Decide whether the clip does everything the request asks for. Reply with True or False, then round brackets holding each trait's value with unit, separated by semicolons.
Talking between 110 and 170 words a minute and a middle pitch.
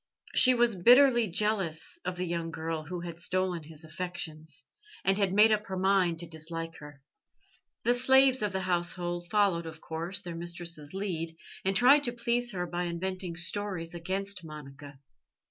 True (165 wpm; 180 Hz)